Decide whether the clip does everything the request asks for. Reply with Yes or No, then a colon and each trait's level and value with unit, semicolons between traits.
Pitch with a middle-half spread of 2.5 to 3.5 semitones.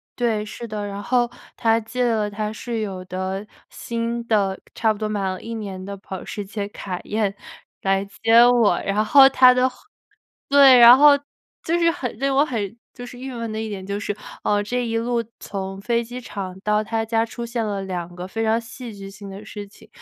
Yes: average, 3.0 semitones